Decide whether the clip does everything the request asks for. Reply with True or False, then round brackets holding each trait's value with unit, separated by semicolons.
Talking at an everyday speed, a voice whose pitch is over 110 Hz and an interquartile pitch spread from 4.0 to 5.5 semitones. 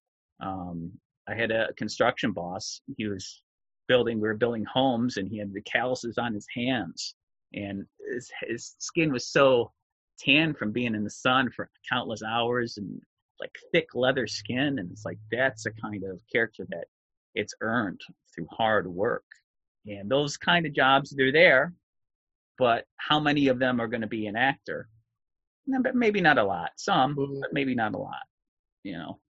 True (175 wpm; 120 Hz; 4.3 semitones)